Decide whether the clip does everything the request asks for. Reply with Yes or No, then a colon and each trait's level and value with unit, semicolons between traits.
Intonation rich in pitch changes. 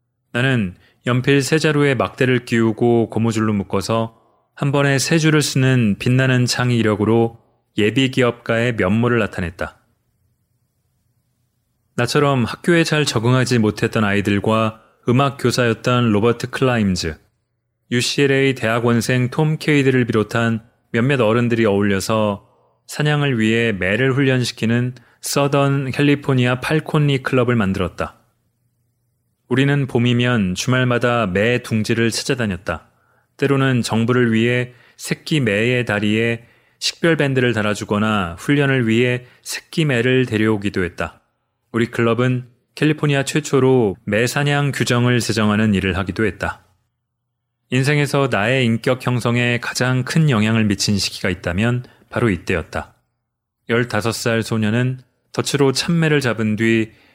No: average, 2.7 semitones